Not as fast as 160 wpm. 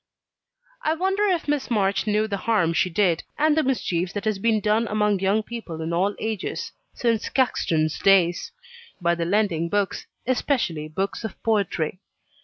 No: average, 165 wpm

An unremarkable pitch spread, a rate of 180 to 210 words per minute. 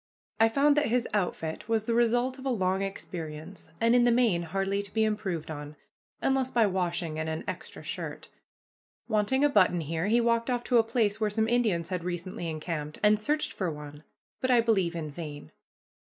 No: wide, 5.7 semitones; average, 195 wpm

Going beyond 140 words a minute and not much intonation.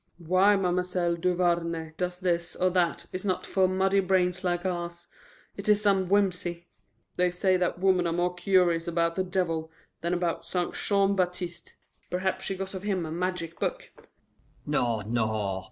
Yes: average, 165 wpm; narrow, 1.6 semitones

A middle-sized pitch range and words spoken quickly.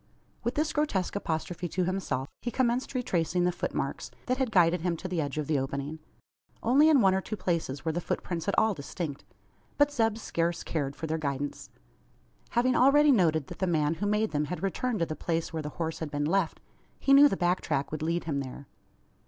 No: wide, 6.0 semitones; fast, 215 wpm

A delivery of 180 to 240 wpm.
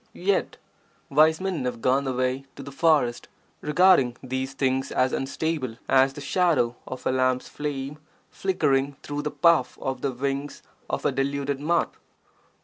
No: average, 150 wpm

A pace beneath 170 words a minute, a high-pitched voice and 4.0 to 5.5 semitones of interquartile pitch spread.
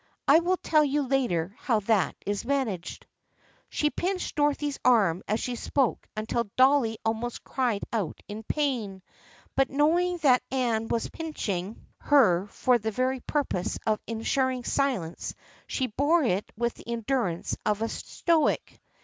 Yes: average, 150 wpm; high, 245 Hz; average, 4.7 semitones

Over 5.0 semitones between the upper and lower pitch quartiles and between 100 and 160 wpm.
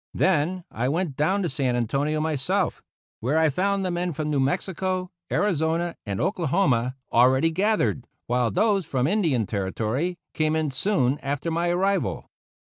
Yes: wide, 5.6 semitones; average, 150 wpm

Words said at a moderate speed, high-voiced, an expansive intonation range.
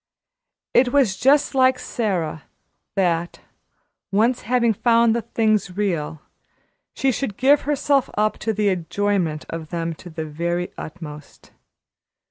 No: slow, 125 wpm; high, 205 Hz; wide, 6.2 semitones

